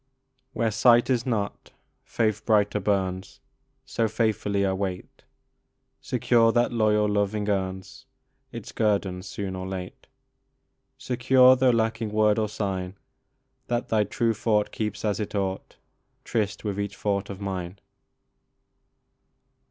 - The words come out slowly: Yes, slow, 125 wpm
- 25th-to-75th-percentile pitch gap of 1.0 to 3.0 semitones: Yes, narrow, 2.6 semitones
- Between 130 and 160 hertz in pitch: No, low, 105 Hz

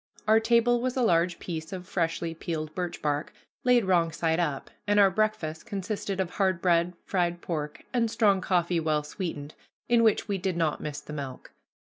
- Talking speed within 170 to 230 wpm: Yes, average, 185 wpm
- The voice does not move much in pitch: No, average, 4.0 semitones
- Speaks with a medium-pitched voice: Yes, medium, 175 Hz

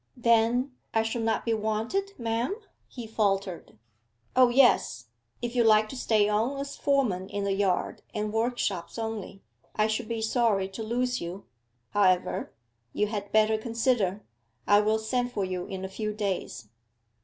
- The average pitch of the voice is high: Yes, high, 220 Hz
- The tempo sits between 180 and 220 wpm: No, average, 160 wpm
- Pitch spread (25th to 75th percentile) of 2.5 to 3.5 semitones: Yes, average, 2.9 semitones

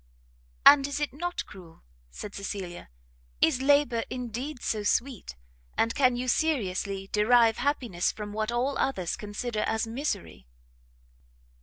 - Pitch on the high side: Yes, high, 230 Hz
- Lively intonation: No, average, 4.7 semitones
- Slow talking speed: Yes, slow, 130 wpm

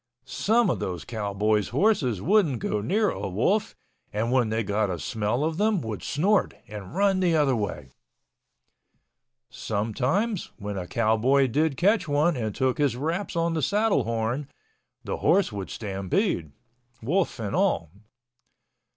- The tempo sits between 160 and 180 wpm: No, average, 150 wpm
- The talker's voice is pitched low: Yes, low, 130 Hz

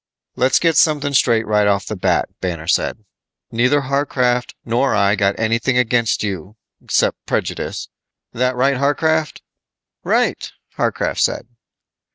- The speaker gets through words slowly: Yes, slow, 130 wpm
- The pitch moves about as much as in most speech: Yes, average, 4.7 semitones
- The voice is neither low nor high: No, low, 120 Hz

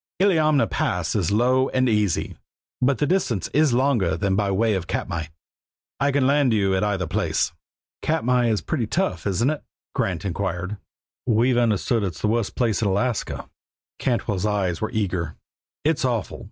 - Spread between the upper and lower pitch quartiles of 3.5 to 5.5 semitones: Yes, average, 5.0 semitones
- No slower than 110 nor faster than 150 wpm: No, average, 165 wpm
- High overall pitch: No, low, 110 Hz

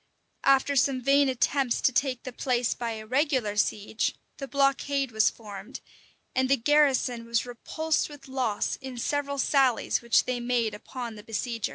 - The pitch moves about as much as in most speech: Yes, average, 3.0 semitones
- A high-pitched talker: Yes, very high, 255 Hz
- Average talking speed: Yes, average, 165 wpm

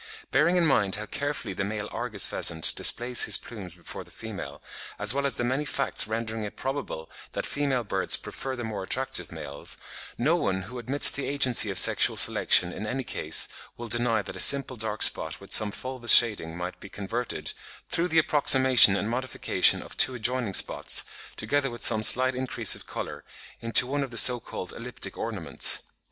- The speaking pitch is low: Yes, low, 120 Hz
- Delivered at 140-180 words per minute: No, average, 190 wpm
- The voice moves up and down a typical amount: Yes, average, 4.2 semitones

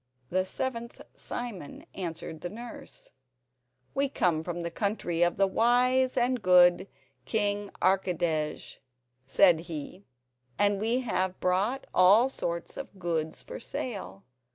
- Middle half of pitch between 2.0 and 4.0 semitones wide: No, average, 5.3 semitones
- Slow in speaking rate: Yes, slow, 125 wpm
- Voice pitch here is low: No, high, 190 Hz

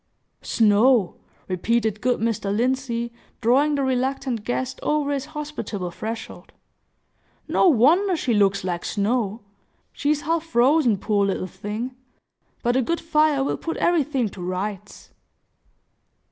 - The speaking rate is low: Yes, slow, 130 wpm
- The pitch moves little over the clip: No, wide, 5.4 semitones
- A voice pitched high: Yes, high, 240 Hz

